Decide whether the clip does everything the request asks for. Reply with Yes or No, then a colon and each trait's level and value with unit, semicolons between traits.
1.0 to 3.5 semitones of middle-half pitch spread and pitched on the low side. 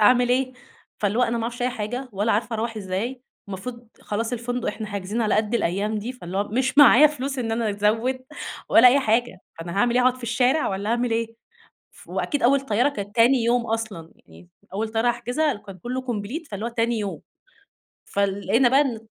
No: average, 3.1 semitones; high, 230 Hz